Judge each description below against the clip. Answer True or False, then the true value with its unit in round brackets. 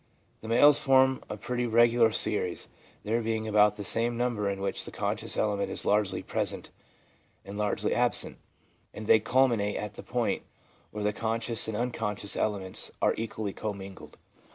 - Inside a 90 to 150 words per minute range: False (160 wpm)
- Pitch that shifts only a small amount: True (2.2 semitones)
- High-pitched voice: False (110 Hz)